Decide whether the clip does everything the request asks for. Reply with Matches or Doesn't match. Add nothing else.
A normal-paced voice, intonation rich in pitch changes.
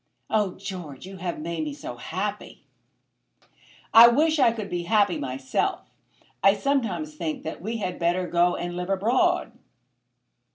Doesn't match